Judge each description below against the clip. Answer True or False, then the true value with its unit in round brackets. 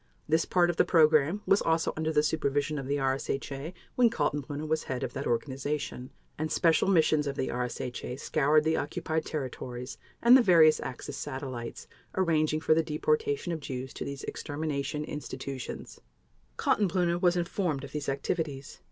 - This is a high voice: False (150 Hz)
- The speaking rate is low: False (160 wpm)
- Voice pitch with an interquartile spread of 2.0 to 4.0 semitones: True (3.0 semitones)